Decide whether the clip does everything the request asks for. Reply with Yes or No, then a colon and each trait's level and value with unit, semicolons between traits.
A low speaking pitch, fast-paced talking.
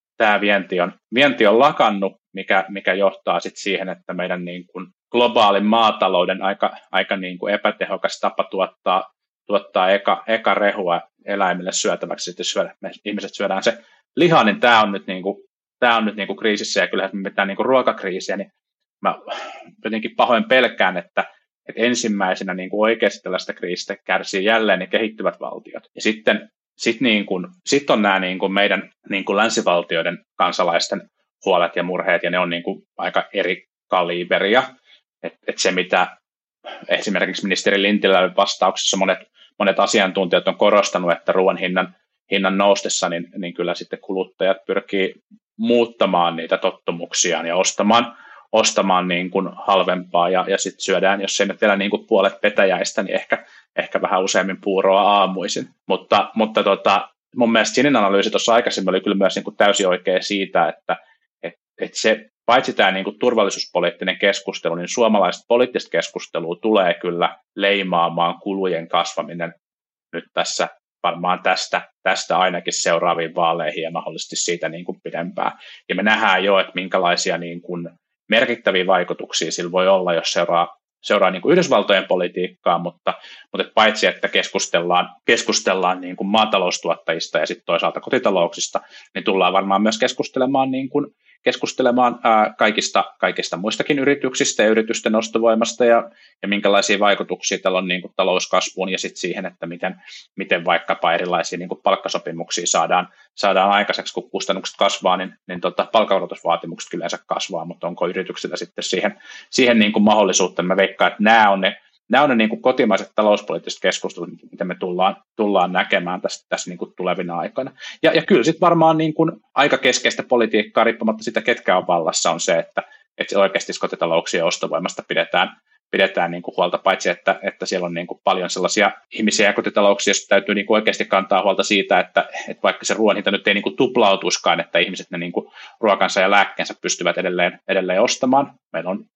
Yes: low, 100 Hz; fast, 165 wpm